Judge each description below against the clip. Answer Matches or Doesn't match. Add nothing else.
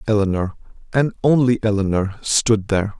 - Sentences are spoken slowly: Matches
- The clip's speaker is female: Doesn't match